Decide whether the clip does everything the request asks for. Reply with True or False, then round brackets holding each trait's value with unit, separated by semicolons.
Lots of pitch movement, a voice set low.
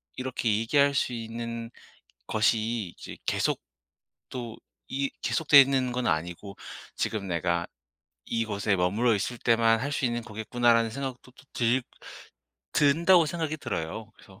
False (3.3 semitones; 115 Hz)